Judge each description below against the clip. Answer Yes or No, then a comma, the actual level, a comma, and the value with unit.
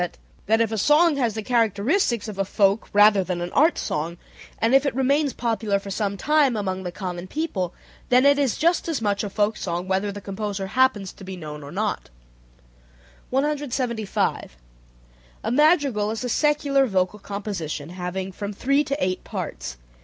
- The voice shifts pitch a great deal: Yes, wide, 5.7 semitones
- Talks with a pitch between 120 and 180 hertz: No, high, 210 Hz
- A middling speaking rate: Yes, average, 175 wpm